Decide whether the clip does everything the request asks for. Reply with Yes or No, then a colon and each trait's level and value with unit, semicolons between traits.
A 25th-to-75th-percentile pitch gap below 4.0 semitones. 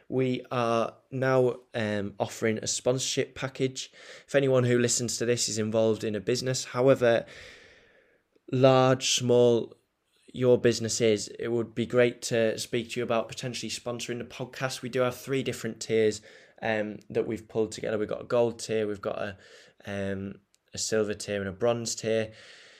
Yes: narrow, 2.6 semitones